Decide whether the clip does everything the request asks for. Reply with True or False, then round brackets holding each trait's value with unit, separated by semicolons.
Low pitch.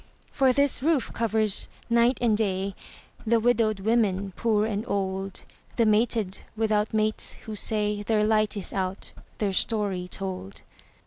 False (215 Hz)